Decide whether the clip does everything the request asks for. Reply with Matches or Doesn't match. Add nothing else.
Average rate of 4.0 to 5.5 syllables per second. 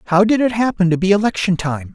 Doesn't match